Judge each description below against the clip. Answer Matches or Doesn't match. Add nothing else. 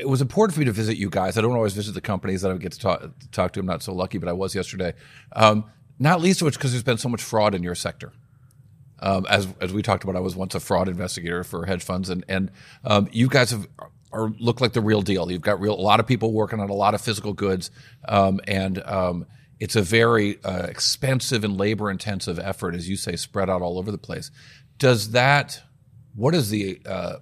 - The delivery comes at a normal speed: Doesn't match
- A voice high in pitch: Doesn't match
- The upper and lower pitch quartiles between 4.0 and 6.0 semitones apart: Matches